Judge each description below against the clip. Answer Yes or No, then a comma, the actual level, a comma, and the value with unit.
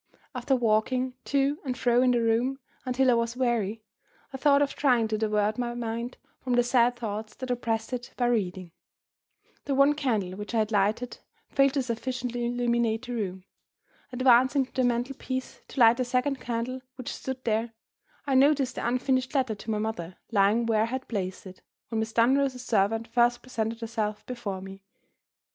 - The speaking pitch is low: No, high, 240 Hz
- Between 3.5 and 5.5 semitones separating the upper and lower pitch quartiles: No, narrow, 2.5 semitones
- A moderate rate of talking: Yes, average, 185 wpm